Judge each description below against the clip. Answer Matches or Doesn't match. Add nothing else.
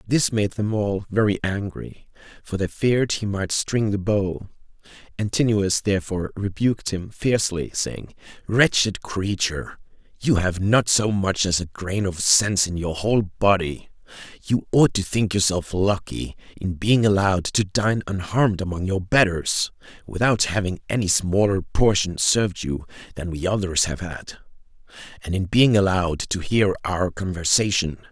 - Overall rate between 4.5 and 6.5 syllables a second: Matches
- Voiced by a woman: Doesn't match